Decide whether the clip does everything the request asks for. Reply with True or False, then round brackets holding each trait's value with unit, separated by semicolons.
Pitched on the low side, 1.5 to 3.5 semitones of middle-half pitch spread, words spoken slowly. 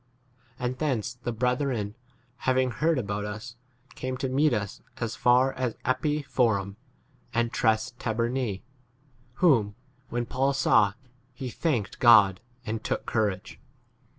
True (120 Hz; 3.1 semitones; 125 wpm)